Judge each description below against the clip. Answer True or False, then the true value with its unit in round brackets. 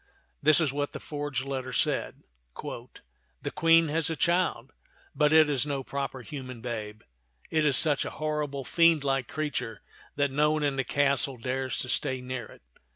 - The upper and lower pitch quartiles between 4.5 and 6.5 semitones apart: False (2.8 semitones)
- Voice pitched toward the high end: False (140 Hz)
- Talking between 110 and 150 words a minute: False (175 wpm)